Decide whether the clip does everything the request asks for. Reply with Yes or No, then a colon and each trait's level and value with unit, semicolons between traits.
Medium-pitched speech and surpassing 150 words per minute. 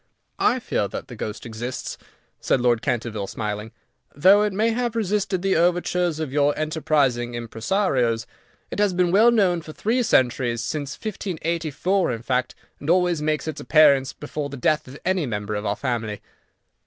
Yes: medium, 150 Hz; average, 165 wpm